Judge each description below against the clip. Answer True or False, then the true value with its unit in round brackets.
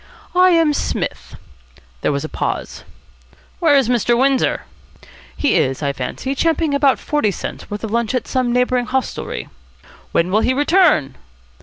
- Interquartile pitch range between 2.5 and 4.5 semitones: False (5.3 semitones)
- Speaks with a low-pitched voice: False (255 Hz)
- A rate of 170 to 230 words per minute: False (155 wpm)